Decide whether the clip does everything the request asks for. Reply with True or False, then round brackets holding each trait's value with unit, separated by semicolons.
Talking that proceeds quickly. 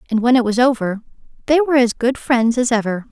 True (230 wpm)